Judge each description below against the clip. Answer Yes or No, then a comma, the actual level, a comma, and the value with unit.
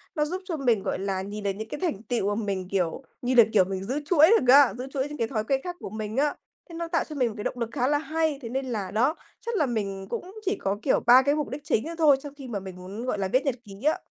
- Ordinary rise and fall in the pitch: No, wide, 6.2 semitones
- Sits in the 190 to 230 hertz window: No, very high, 250 Hz